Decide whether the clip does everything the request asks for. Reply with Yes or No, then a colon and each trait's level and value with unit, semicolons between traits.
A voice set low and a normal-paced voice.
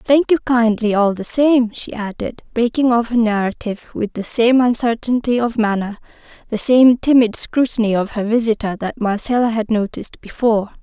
No: high, 230 Hz; average, 165 wpm